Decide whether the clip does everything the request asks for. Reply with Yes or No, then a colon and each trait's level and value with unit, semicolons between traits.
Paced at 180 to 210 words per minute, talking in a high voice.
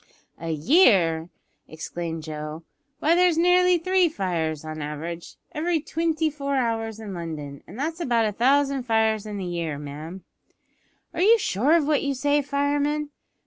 No: average, 160 wpm; high, 230 Hz